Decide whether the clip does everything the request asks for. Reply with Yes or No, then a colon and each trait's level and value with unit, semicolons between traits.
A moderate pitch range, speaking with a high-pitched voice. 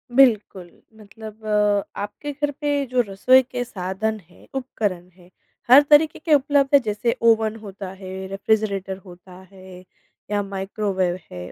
Yes: average, 4.8 semitones; high, 210 Hz